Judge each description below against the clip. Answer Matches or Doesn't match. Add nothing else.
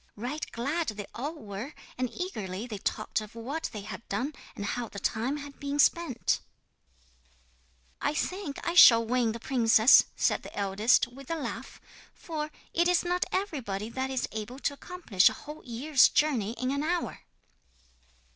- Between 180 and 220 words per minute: Doesn't match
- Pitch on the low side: Doesn't match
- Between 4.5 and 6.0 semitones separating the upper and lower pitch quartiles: Matches